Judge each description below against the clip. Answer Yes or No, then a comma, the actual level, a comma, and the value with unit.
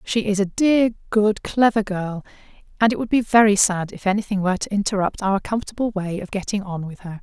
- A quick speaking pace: Yes, fast, 215 wpm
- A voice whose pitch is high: Yes, high, 205 Hz